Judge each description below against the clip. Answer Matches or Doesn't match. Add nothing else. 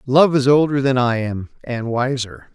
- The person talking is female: Doesn't match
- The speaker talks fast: Doesn't match